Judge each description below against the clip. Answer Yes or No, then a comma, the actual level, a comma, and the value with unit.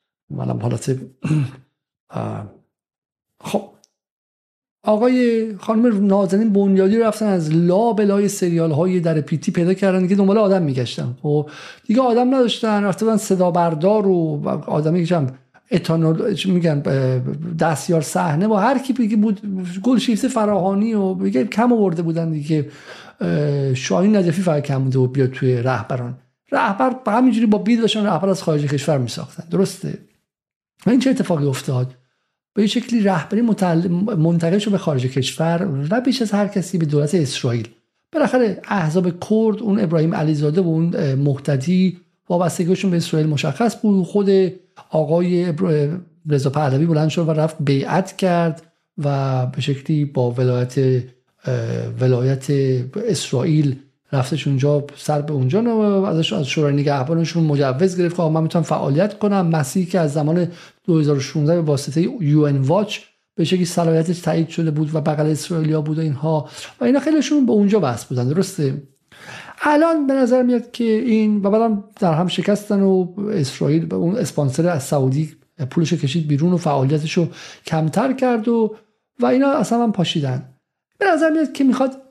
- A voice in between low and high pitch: Yes, medium, 170 Hz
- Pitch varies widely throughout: Yes, wide, 5.7 semitones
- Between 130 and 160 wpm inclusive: Yes, average, 150 wpm